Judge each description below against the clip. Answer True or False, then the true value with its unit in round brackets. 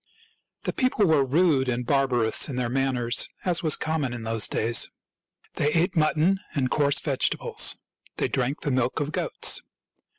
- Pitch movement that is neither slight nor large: True (4.0 semitones)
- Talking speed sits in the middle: True (160 wpm)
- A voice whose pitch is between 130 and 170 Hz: True (135 Hz)